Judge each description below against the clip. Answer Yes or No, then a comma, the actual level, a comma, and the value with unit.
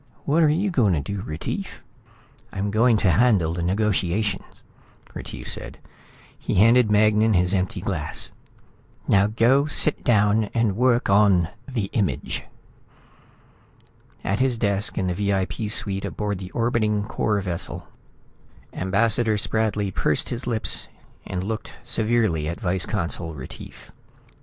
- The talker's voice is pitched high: No, low, 105 Hz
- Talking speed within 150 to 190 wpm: No, slow, 135 wpm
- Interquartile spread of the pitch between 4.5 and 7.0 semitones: No, average, 3.4 semitones